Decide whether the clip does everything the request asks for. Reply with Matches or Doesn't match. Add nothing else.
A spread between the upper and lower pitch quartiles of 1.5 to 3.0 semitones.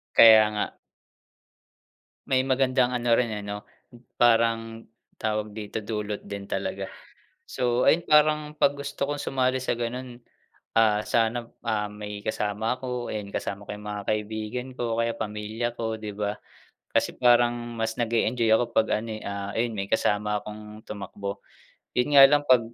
Matches